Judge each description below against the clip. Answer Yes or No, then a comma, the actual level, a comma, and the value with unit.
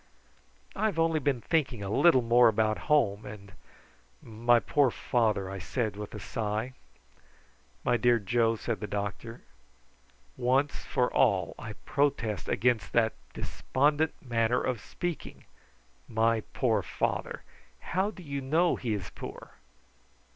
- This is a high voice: No, low, 120 Hz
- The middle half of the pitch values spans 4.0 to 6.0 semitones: Yes, average, 4.4 semitones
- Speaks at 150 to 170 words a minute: No, slow, 135 wpm